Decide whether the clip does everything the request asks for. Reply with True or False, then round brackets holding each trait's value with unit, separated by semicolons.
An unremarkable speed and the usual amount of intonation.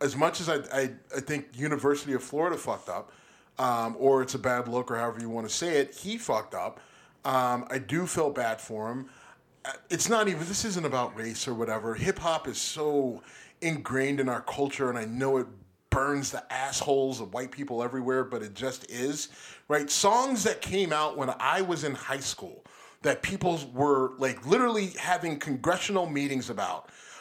True (190 wpm; 4.4 semitones)